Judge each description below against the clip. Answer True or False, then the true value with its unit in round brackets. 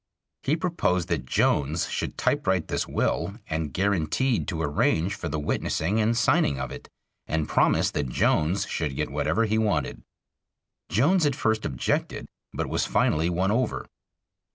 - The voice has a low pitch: True (90 Hz)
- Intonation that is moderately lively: False (6.1 semitones)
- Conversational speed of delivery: True (155 wpm)